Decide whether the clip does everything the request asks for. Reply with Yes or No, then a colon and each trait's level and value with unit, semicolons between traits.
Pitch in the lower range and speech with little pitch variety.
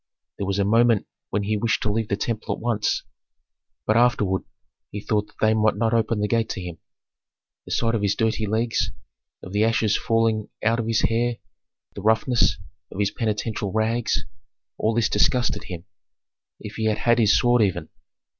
Yes: low, 110 Hz; narrow, 1.8 semitones